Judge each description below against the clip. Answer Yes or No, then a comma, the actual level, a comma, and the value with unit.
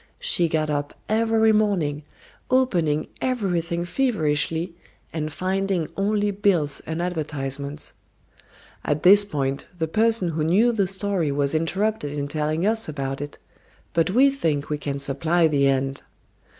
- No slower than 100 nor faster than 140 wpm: Yes, slow, 135 wpm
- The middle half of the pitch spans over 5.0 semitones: Yes, wide, 5.6 semitones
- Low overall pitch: No, medium, 165 Hz